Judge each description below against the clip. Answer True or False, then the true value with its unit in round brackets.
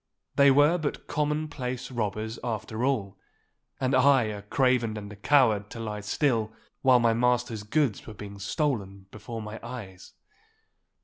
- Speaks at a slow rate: False (150 wpm)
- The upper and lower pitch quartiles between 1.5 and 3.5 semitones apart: False (3.9 semitones)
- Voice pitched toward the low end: True (115 Hz)